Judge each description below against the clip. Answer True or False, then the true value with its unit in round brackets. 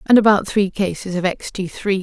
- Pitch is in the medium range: False (195 Hz)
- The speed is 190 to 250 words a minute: True (205 wpm)